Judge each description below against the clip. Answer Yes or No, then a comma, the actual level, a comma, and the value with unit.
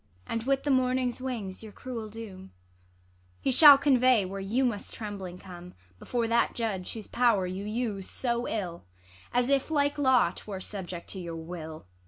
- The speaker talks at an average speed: Yes, average, 175 wpm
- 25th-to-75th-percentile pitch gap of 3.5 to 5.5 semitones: Yes, average, 5.0 semitones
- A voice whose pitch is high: Yes, high, 225 Hz